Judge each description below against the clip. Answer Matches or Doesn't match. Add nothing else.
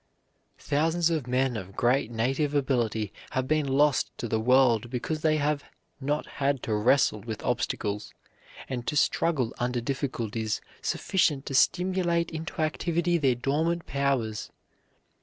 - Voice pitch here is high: Doesn't match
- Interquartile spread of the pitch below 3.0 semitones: Doesn't match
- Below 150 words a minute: Matches